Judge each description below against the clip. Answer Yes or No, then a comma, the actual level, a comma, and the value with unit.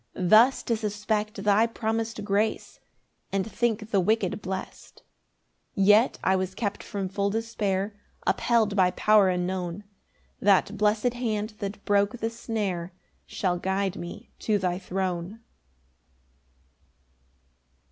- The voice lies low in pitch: No, high, 205 Hz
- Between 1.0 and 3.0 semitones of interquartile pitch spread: Yes, narrow, 2.5 semitones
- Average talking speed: No, slow, 120 wpm